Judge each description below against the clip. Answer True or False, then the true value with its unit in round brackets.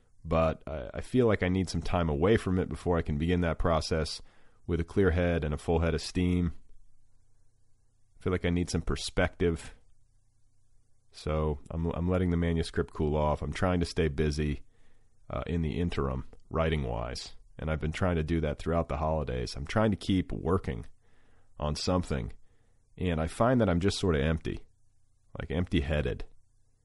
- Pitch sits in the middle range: False (85 Hz)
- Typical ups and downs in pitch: True (4.5 semitones)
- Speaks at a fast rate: False (185 wpm)